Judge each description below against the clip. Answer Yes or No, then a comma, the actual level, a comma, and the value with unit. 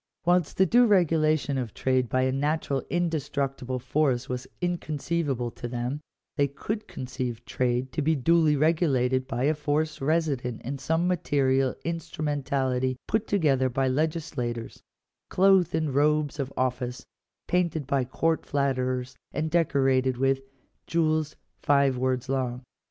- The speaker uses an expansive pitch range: No, average, 3.6 semitones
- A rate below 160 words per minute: Yes, average, 140 wpm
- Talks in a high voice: No, medium, 140 Hz